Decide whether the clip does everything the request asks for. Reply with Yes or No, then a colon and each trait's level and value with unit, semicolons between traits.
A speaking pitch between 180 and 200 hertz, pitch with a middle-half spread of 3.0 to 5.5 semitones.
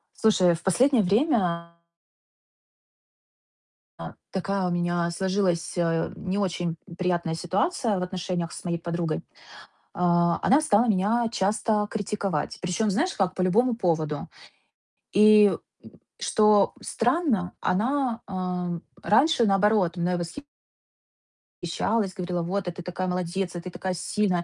Yes: medium, 185 Hz; average, 3.4 semitones